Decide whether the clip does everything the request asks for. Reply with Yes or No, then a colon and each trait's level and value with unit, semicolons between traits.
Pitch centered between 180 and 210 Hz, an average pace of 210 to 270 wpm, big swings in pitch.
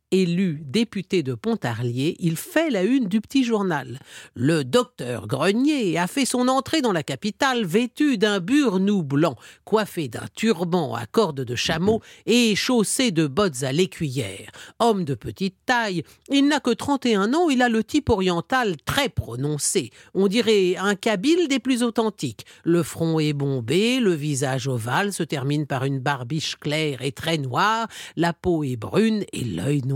No: medium, 185 Hz; average, 170 wpm; wide, 7.7 semitones